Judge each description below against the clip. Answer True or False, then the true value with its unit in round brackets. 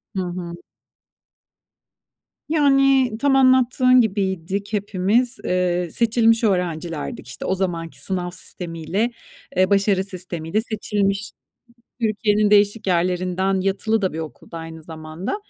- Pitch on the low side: False (195 Hz)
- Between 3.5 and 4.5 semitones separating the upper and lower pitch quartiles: True (4.0 semitones)